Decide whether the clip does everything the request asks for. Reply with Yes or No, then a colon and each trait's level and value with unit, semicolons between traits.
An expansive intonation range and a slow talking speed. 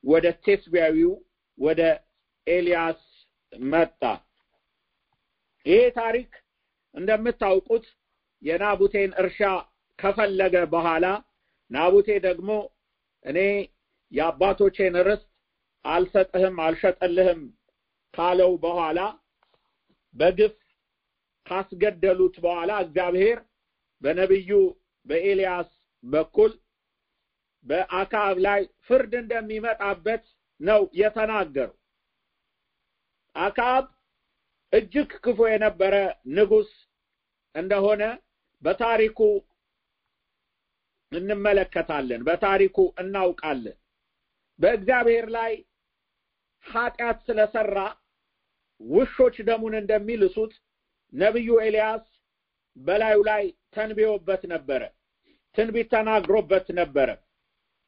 No: average, 3.7 semitones; slow, 60 wpm